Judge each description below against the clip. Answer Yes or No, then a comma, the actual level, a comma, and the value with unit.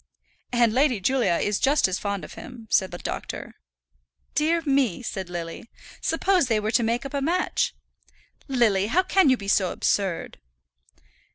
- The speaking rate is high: No, average, 165 wpm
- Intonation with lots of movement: Yes, wide, 5.7 semitones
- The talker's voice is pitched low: No, high, 235 Hz